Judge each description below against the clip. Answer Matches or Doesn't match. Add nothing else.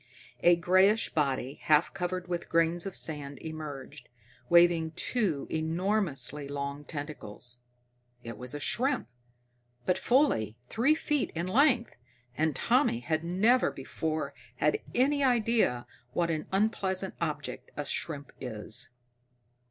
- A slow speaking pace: Matches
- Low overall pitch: Doesn't match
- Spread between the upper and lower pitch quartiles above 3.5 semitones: Matches